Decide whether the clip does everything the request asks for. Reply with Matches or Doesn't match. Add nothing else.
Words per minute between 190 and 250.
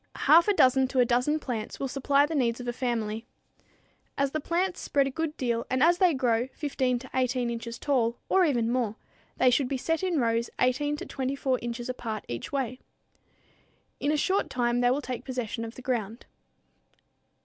Matches